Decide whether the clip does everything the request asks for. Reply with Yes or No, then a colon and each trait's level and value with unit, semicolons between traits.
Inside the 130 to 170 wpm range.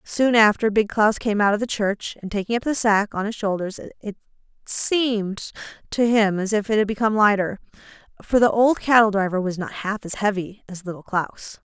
No: fast, 205 wpm